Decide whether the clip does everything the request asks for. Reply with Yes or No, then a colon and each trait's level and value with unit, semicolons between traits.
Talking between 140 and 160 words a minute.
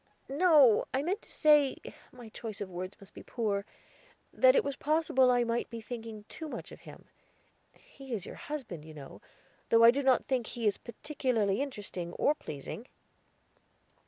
No: average, 175 wpm